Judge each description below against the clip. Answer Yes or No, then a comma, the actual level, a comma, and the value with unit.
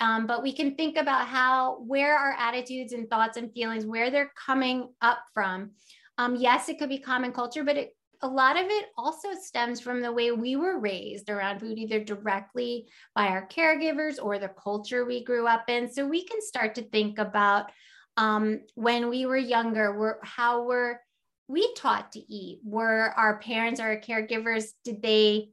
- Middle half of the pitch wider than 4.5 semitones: No, average, 3.2 semitones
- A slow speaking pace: No, average, 190 wpm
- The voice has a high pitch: Yes, high, 240 Hz